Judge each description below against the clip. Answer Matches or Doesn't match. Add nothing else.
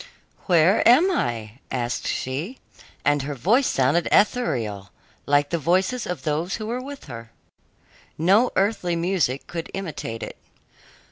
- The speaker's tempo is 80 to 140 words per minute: Matches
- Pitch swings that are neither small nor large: Doesn't match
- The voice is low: Doesn't match